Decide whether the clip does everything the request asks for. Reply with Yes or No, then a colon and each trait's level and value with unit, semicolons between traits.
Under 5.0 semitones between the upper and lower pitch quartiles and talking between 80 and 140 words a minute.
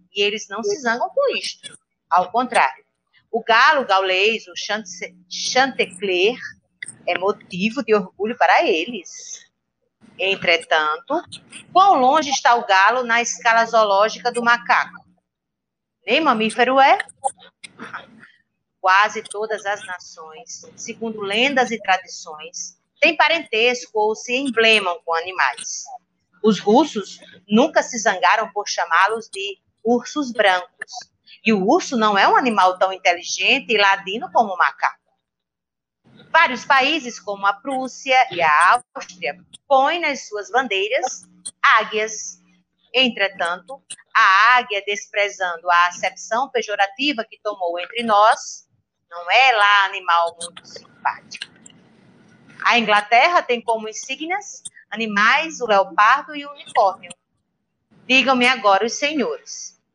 No: average, 5.3 semitones; slow, 120 wpm